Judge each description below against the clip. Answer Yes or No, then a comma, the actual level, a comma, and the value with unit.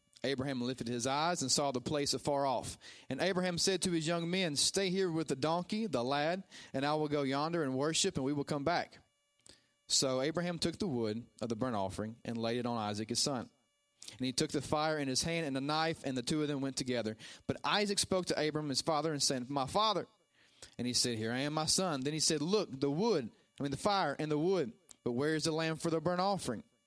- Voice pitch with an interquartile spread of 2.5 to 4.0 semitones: No, average, 4.4 semitones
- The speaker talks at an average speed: No, fast, 250 wpm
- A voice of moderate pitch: Yes, medium, 145 Hz